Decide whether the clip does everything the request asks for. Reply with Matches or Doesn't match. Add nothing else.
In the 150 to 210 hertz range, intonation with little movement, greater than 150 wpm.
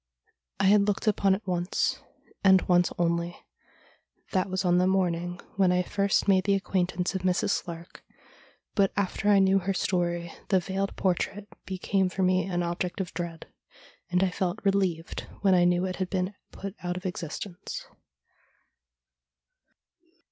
Matches